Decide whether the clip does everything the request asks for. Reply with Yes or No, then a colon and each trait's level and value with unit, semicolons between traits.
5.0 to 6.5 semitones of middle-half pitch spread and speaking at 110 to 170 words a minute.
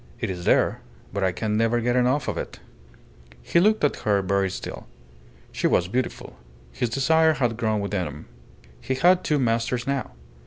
No: wide, 5.4 semitones; average, 180 wpm